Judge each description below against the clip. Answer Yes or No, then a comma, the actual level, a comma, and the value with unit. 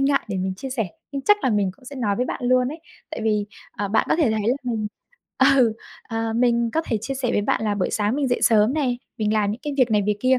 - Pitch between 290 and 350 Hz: No, high, 230 Hz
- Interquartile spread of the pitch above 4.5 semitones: No, average, 3.7 semitones